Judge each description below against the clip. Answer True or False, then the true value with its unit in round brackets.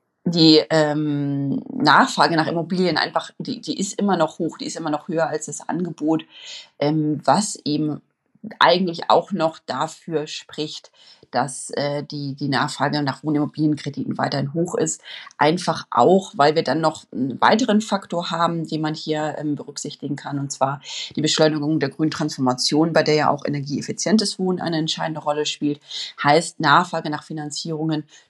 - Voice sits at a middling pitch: True (155 Hz)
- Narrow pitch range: True (2.3 semitones)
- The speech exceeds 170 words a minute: False (155 wpm)